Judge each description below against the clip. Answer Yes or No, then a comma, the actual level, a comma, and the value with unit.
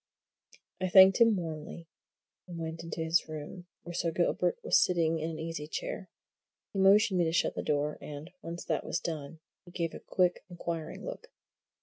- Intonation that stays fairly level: Yes, narrow, 2.1 semitones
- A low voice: No, medium, 170 Hz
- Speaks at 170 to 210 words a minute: Yes, average, 185 wpm